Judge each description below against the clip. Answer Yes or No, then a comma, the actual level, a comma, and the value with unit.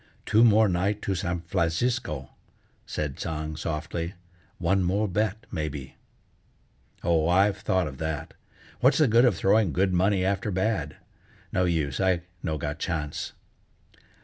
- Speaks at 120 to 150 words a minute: Yes, average, 140 wpm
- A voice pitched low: Yes, very low, 90 Hz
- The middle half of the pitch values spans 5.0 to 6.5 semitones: No, average, 4.2 semitones